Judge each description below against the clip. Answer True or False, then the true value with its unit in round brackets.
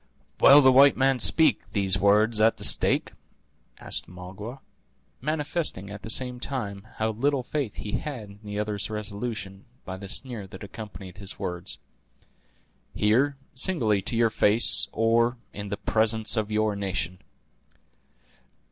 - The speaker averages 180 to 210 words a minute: False (145 wpm)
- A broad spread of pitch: False (3.8 semitones)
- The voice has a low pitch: True (110 Hz)